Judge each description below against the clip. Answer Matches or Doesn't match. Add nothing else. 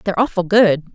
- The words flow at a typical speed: Matches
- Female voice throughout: Matches